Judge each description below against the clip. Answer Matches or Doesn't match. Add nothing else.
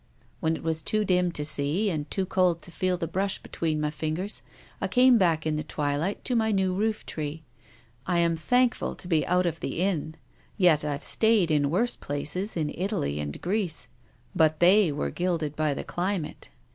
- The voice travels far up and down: Doesn't match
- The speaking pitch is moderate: Matches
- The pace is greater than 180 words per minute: Matches